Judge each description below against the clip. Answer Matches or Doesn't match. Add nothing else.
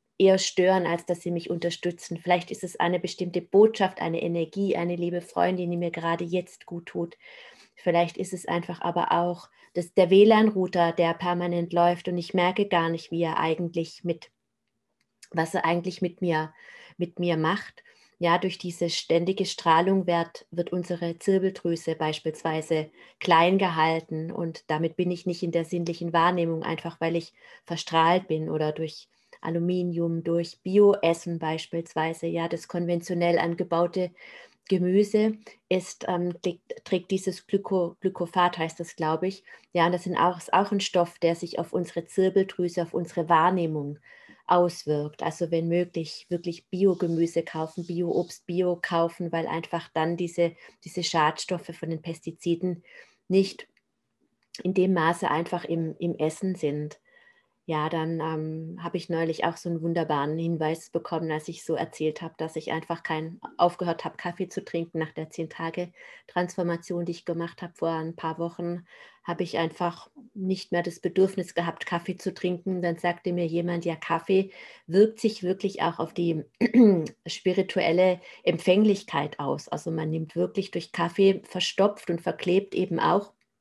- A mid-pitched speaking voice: Matches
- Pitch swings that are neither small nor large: Doesn't match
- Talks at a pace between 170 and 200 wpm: Doesn't match